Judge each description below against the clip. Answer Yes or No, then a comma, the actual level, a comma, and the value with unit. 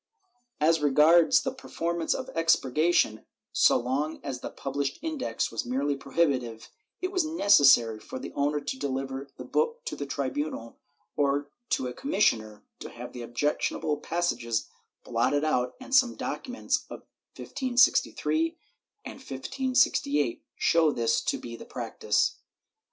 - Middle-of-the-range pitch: Yes, medium, 145 Hz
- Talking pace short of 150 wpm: Yes, average, 140 wpm